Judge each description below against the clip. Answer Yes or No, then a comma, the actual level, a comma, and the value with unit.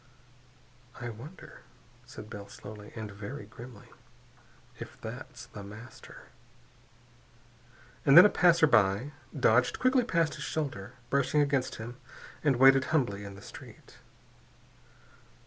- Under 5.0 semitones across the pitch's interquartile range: No, wide, 5.4 semitones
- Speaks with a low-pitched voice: Yes, low, 125 Hz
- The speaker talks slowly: Yes, slow, 115 wpm